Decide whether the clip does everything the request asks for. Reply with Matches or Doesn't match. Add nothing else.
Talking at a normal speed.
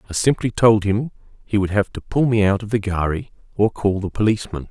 Doesn't match